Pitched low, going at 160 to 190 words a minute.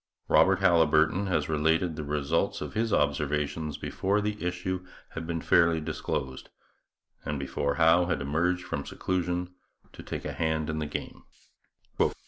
No: very low, 80 Hz; average, 145 wpm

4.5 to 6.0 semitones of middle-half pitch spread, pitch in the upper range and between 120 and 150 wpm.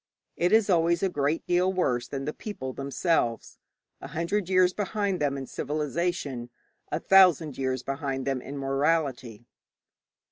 No: average, 4.8 semitones; medium, 150 Hz; average, 145 wpm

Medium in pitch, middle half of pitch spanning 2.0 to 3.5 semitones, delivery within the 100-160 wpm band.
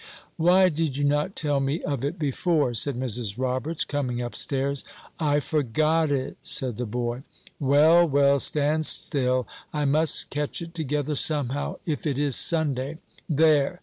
Yes: medium, 145 Hz; average, 3.0 semitones; average, 155 wpm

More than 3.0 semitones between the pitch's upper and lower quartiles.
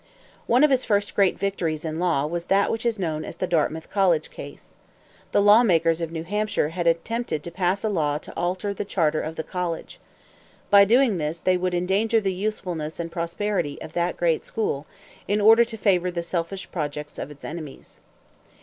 Yes: average, 3.9 semitones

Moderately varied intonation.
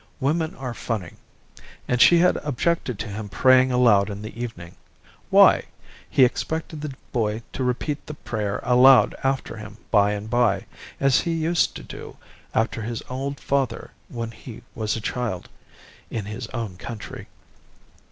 Yes: average, 4.0 semitones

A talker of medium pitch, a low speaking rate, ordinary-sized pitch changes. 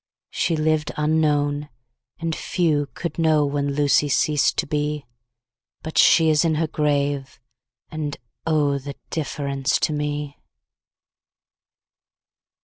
No: medium, 150 Hz; slow, 120 wpm; narrow, 1.5 semitones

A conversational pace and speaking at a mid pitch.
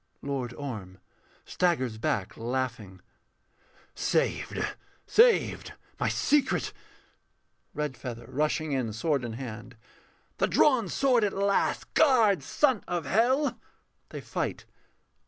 No: slow, 105 wpm; medium, 145 Hz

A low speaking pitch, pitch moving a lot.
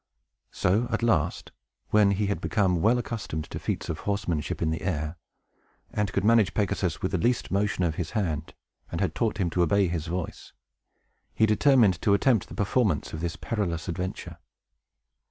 No: very low, 95 Hz; average, 4.0 semitones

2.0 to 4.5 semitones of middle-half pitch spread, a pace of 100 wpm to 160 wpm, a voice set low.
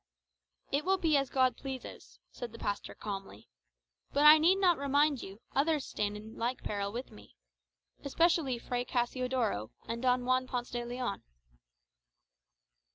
No: average, 3.6 semitones; average, 150 wpm; very high, 255 Hz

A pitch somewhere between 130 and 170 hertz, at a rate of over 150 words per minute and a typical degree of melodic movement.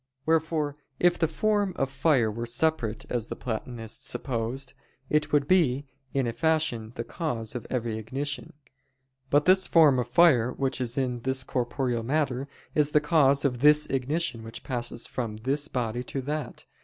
Yes: low, 135 Hz; average, 165 wpm; average, 4.1 semitones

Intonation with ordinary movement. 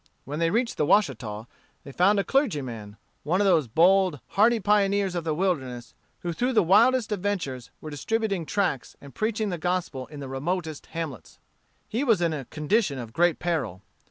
No: wide, 6.3 semitones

